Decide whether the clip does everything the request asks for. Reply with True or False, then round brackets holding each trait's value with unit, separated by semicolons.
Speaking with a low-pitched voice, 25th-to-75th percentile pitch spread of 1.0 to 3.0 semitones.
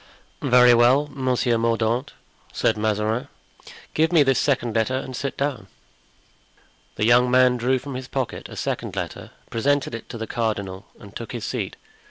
True (125 Hz; 2.6 semitones)